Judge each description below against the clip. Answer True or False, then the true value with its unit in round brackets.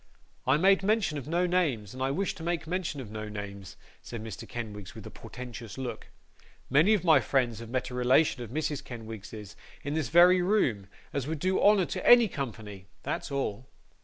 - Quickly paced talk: False (195 wpm)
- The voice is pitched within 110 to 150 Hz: True (135 Hz)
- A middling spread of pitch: False (7.5 semitones)